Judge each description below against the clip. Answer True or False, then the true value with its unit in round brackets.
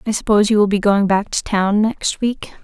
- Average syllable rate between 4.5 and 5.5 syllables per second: True (5.3 syllables/s)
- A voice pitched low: False (205 Hz)